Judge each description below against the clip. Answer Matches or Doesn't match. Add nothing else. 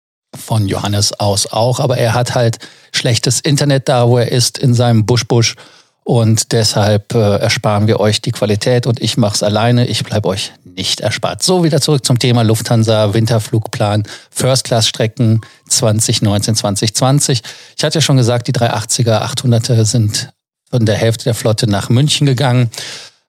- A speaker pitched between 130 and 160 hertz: Doesn't match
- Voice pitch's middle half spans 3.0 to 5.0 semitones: Doesn't match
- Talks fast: Doesn't match